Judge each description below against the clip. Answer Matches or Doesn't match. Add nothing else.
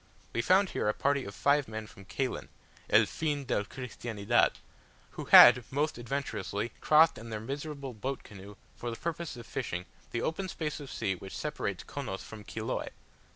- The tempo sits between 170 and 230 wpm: Matches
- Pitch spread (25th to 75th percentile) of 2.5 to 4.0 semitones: Doesn't match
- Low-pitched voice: Matches